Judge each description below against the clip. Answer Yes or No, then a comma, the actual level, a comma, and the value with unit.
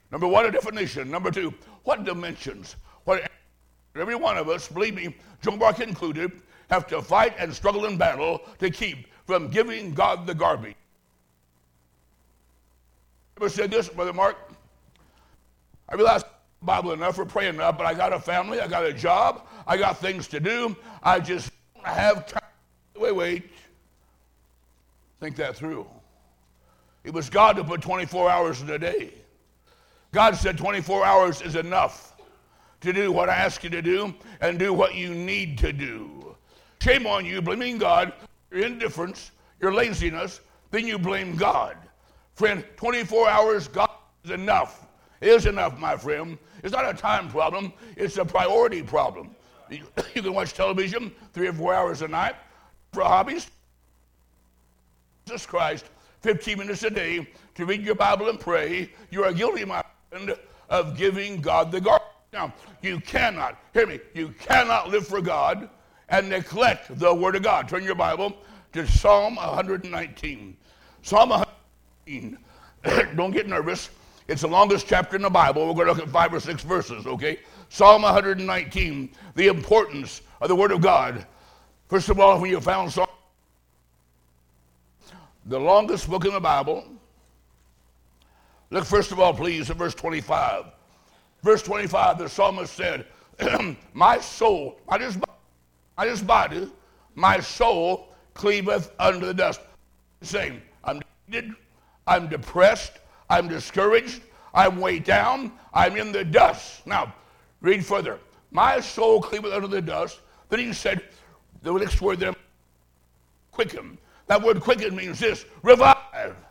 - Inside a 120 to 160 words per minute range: Yes, average, 150 wpm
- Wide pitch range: Yes, wide, 7.6 semitones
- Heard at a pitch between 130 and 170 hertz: No, medium, 185 Hz